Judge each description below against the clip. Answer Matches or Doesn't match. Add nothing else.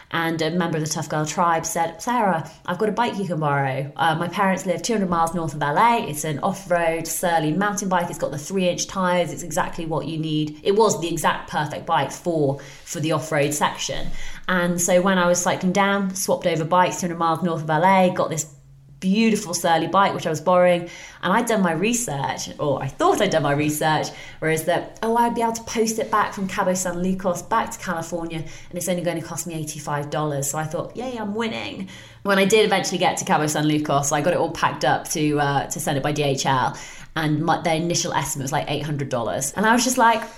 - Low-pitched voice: Doesn't match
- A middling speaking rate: Doesn't match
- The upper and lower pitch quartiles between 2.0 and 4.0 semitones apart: Matches